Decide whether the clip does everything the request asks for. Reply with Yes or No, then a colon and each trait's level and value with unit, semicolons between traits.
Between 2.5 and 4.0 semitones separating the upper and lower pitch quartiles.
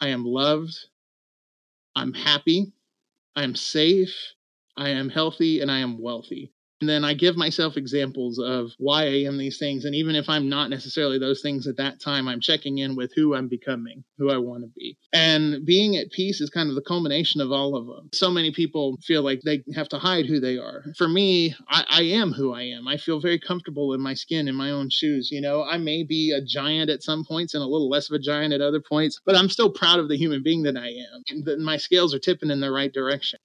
Yes: average, 2.9 semitones